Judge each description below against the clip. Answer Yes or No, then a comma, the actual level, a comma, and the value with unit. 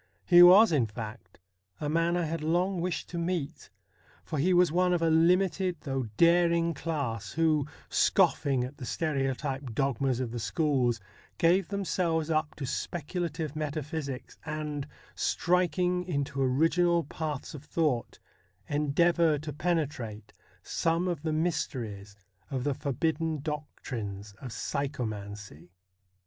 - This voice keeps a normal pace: No, slow, 130 wpm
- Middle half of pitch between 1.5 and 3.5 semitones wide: No, average, 4.1 semitones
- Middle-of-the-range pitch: Yes, medium, 155 Hz